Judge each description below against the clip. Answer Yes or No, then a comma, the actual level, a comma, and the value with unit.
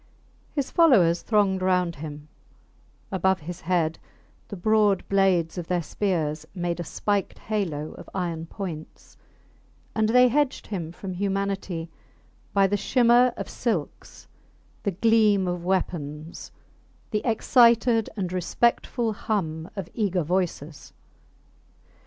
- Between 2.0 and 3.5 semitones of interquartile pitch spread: No, average, 4.0 semitones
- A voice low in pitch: No, high, 190 Hz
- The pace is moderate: No, slow, 120 wpm